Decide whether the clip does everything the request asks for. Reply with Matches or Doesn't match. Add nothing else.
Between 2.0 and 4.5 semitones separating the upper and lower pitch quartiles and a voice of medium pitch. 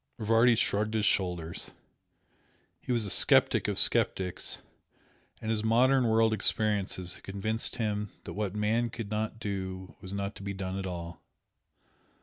Doesn't match